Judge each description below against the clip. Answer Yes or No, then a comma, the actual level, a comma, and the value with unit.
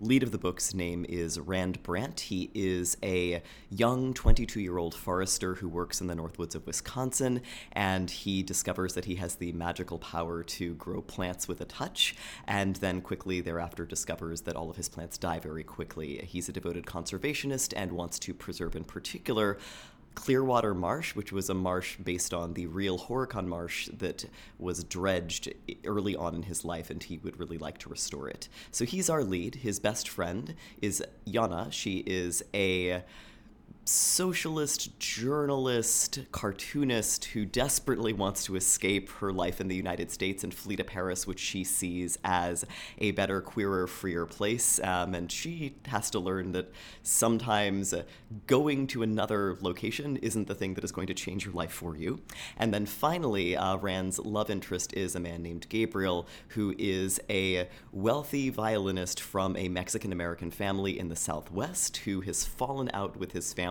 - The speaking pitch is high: No, very low, 95 Hz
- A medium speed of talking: Yes, average, 170 wpm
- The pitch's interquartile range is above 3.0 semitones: Yes, average, 3.5 semitones